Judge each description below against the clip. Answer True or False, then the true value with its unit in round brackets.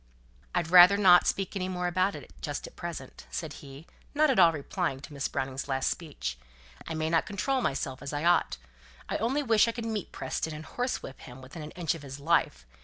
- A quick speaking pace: True (215 wpm)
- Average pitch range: False (5.7 semitones)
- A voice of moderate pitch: True (165 Hz)